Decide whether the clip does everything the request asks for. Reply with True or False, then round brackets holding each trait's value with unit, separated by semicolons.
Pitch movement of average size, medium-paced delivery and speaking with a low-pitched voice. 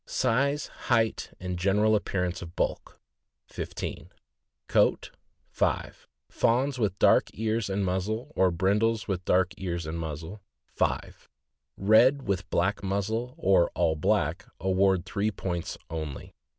False (3.7 semitones; 130 wpm; 95 Hz)